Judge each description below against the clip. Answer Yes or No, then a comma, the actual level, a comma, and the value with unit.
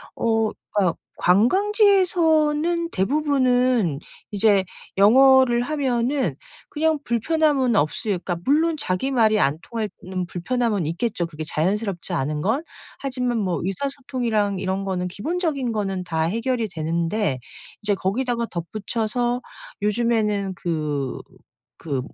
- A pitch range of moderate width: No, wide, 6.1 semitones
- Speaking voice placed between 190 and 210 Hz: No, high, 220 Hz